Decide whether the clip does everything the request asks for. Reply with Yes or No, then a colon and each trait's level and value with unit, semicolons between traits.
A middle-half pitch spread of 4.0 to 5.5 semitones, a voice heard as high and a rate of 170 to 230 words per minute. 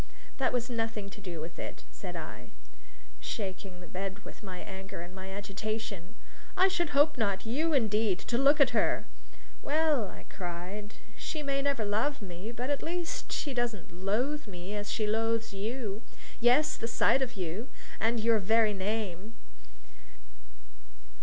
No: average, 4.7 semitones; high, 220 Hz; average, 160 wpm